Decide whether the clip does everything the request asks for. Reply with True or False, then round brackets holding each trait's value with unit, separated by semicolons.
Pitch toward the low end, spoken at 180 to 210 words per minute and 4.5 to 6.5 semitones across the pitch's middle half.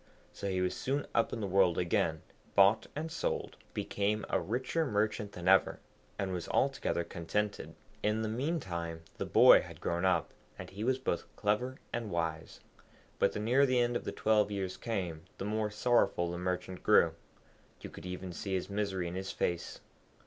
False (100 Hz; 185 wpm; 3.8 semitones)